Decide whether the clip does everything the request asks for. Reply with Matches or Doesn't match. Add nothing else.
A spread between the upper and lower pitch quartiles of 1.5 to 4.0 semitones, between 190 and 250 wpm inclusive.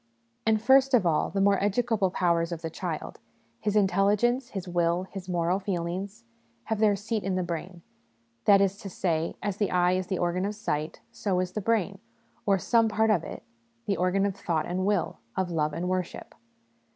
Matches